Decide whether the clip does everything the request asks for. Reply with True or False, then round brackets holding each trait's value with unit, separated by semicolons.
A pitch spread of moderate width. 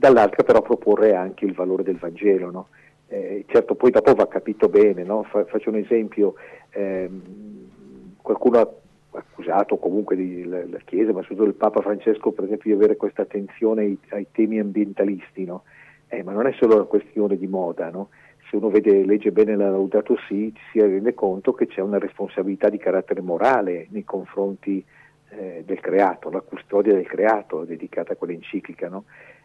False (2.2 semitones)